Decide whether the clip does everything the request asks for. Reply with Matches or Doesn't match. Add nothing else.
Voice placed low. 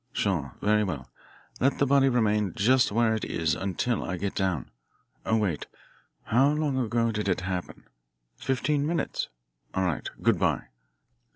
Matches